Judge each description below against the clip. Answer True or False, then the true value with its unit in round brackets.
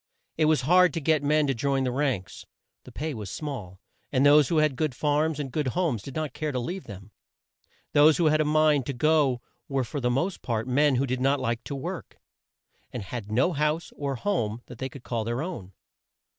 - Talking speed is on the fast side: True (220 wpm)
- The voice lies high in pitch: False (140 Hz)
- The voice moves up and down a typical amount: True (3.9 semitones)